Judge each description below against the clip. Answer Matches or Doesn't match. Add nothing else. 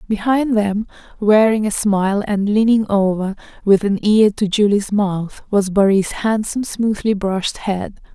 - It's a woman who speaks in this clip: Matches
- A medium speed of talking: Matches